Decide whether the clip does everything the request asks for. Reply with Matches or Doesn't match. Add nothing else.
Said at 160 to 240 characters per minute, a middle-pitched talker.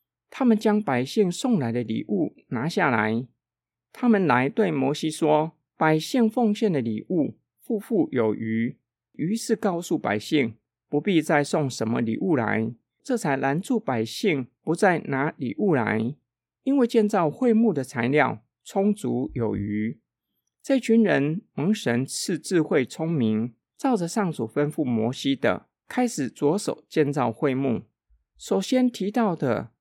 Matches